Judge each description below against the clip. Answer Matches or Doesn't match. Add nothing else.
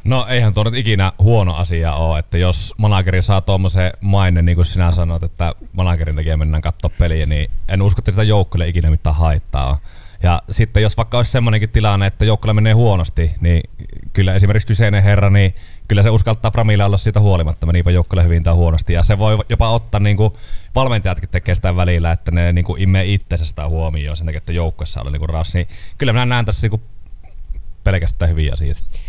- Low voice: Matches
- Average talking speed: Doesn't match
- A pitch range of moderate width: Matches